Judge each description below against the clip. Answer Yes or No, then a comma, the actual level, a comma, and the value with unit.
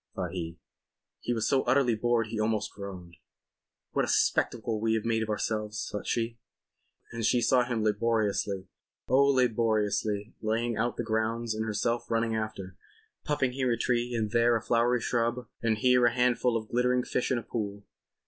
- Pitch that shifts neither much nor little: No, narrow, 2.0 semitones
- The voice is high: No, low, 115 Hz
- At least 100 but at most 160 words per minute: No, average, 170 wpm